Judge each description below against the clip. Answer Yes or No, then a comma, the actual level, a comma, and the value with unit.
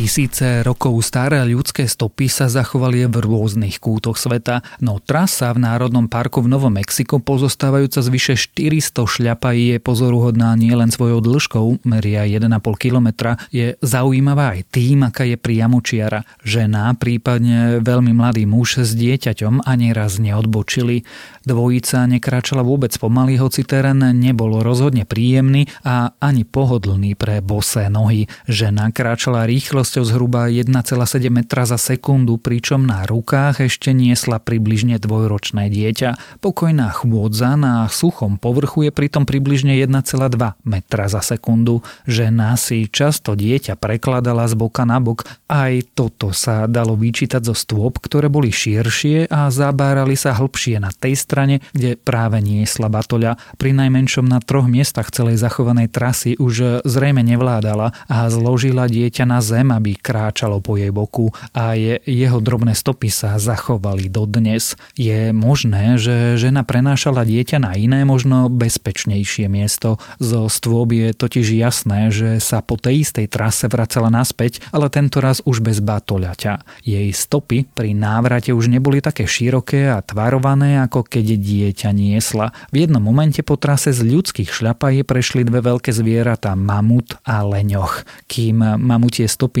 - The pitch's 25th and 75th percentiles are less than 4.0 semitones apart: Yes, average, 2.8 semitones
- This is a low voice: Yes, low, 120 Hz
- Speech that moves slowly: No, average, 145 wpm